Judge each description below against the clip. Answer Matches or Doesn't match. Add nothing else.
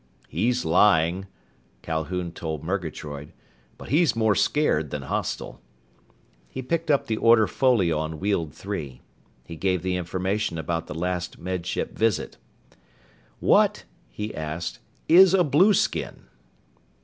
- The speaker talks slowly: Matches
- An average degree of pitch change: Doesn't match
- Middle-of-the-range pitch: Doesn't match